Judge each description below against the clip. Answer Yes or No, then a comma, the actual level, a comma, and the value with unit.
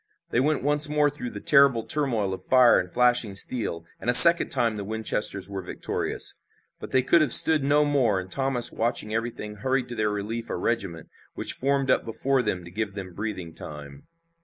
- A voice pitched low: Yes, low, 115 Hz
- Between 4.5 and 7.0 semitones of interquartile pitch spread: Yes, average, 5.2 semitones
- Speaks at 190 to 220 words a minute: Yes, average, 200 wpm